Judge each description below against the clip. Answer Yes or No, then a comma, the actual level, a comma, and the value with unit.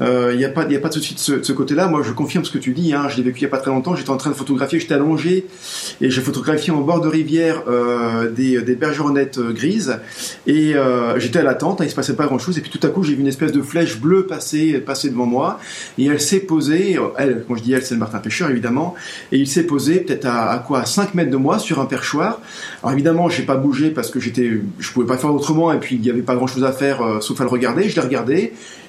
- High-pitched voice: No, medium, 140 Hz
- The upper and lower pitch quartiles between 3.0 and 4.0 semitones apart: Yes, average, 3.6 semitones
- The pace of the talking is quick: Yes, fast, 290 wpm